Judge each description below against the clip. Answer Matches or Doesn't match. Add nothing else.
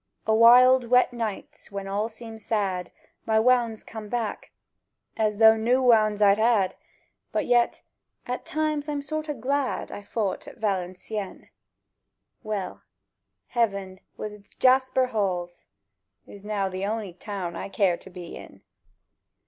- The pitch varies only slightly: Doesn't match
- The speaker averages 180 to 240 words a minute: Doesn't match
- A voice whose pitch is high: Matches